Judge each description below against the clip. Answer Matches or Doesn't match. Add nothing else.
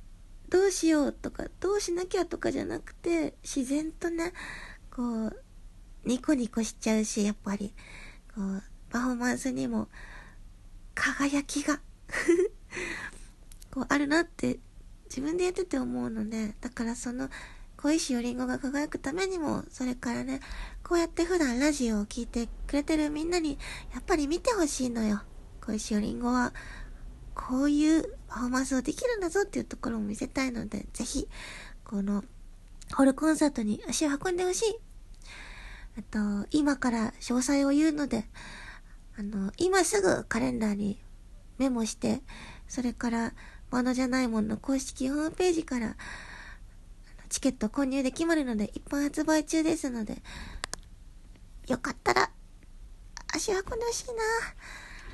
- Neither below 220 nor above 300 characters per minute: Matches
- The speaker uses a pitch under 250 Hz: Doesn't match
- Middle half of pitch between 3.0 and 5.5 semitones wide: Matches